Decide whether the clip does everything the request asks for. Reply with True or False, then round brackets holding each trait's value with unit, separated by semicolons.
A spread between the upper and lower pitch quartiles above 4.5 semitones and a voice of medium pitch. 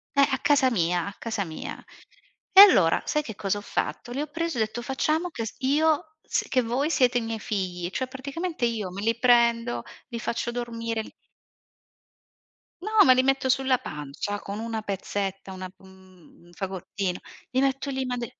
False (5.3 semitones; 235 Hz)